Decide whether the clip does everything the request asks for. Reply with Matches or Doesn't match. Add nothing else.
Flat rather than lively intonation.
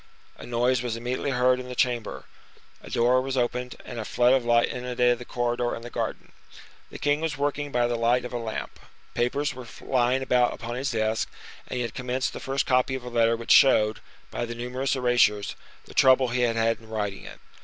Matches